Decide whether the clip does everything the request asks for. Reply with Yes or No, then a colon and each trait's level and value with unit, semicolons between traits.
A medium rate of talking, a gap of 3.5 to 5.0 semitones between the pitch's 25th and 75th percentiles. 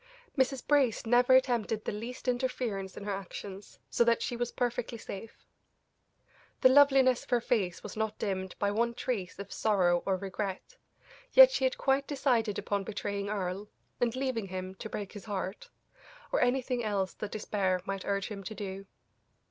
Yes: average, 170 wpm; average, 4.1 semitones